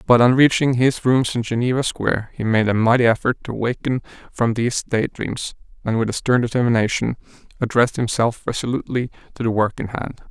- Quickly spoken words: No, average, 185 wpm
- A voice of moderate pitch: No, low, 120 Hz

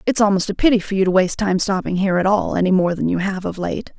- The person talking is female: Yes, female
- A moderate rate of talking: No, fast, 300 wpm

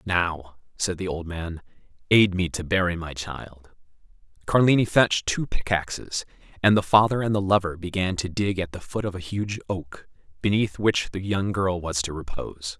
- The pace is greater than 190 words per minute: No, average, 185 wpm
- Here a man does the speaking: Yes, male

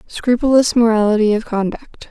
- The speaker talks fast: No, slow, 115 wpm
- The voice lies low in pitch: No, high, 225 Hz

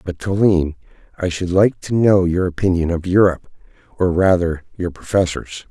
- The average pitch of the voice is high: No, very low, 90 Hz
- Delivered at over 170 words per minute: No, average, 160 wpm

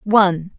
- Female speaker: Yes, female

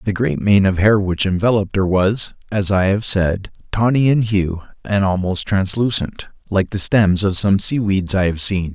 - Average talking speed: Yes, average, 190 wpm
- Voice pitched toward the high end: No, low, 100 Hz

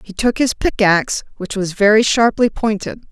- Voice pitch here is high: Yes, high, 210 Hz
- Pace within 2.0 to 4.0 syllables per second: No, 4.9 syllables/s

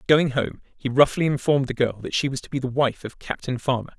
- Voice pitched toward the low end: Yes, low, 130 Hz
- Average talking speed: No, fast, 255 wpm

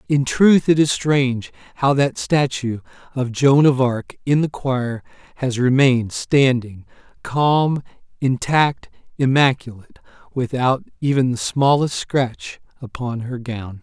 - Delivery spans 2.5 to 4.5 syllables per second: Yes, 4.0 syllables/s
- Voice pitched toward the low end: Yes, low, 130 Hz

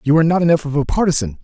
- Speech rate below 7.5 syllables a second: No, 8.3 syllables/s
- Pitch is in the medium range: Yes, medium, 155 Hz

